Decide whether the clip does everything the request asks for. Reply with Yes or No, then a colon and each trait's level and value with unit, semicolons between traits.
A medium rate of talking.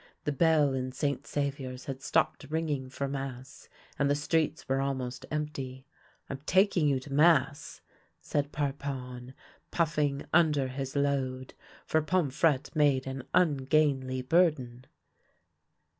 No: slow, 130 wpm